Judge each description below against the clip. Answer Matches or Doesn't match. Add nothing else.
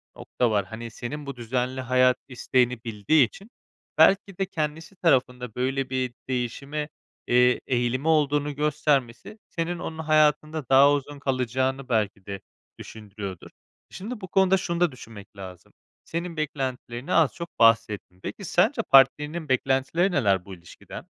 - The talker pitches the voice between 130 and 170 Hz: Matches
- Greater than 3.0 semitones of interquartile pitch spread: Matches